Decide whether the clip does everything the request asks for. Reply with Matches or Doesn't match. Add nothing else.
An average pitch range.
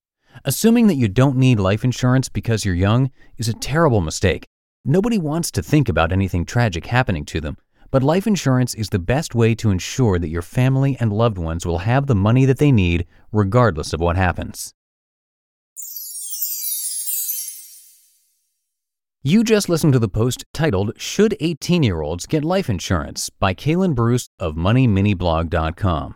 Doesn't match